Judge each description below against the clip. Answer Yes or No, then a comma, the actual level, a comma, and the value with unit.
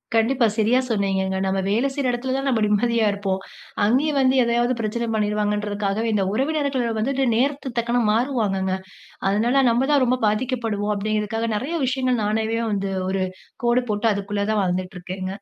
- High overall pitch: Yes, high, 225 Hz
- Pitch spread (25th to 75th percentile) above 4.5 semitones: No, average, 3.6 semitones